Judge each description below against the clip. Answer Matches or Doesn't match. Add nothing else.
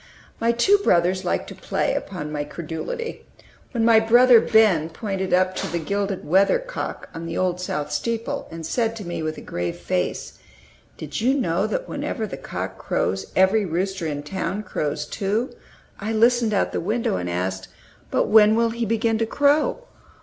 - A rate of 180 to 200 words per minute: Matches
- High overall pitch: Matches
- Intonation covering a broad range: Matches